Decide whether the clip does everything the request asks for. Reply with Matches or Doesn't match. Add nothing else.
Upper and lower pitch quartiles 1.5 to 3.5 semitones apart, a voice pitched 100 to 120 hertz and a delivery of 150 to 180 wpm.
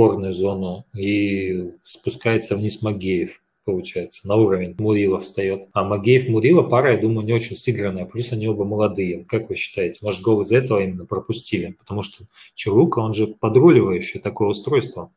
Matches